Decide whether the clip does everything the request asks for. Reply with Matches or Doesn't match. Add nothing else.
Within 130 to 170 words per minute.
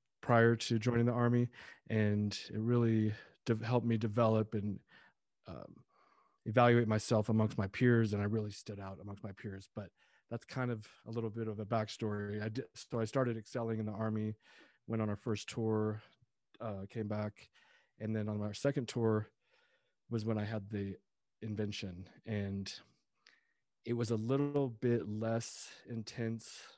Matches